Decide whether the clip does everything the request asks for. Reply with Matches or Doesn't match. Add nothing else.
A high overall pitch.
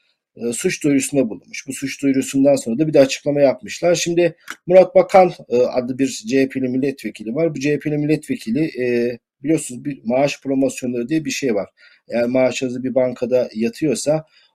Doesn't match